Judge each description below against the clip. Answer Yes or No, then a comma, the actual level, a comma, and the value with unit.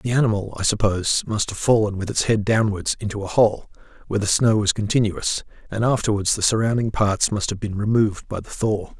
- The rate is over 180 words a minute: Yes, fast, 205 wpm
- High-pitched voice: No, low, 105 Hz